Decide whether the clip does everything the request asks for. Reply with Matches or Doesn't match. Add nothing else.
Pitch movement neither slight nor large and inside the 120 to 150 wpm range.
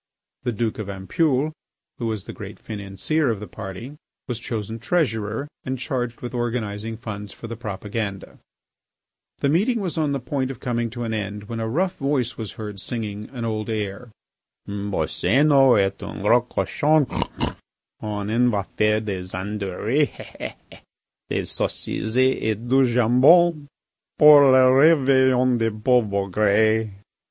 Matches